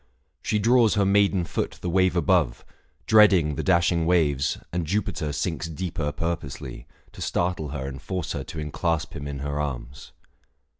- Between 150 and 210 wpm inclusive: Yes, average, 160 wpm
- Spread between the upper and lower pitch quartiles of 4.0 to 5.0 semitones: Yes, average, 4.3 semitones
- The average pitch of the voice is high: No, very low, 85 Hz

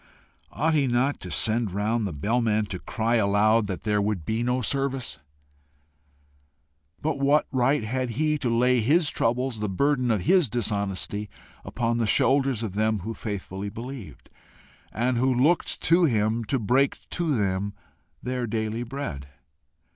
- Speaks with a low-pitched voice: Yes, low, 115 Hz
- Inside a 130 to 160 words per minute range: Yes, average, 155 wpm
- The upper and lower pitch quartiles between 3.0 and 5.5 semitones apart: Yes, average, 4.0 semitones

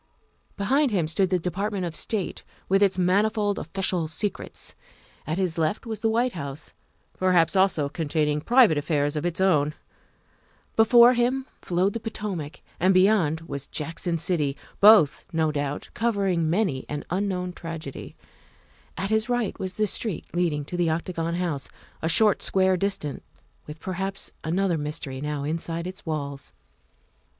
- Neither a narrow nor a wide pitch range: Yes, average, 4.2 semitones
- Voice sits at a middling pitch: Yes, medium, 180 Hz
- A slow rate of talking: No, average, 150 wpm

